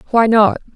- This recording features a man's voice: No, female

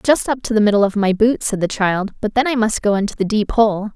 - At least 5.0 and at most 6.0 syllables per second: Yes, 5.7 syllables/s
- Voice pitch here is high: Yes, high, 215 Hz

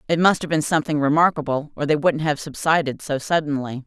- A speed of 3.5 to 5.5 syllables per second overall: No, 6.0 syllables/s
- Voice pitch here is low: No, medium, 150 Hz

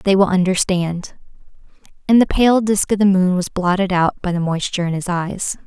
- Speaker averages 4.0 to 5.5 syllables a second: Yes, 5.1 syllables/s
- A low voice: No, medium, 185 Hz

